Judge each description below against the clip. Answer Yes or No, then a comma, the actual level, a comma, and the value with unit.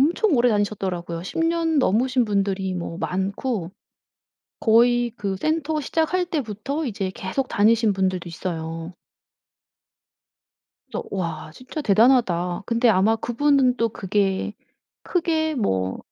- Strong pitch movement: Yes, wide, 6.0 semitones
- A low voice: No, high, 215 Hz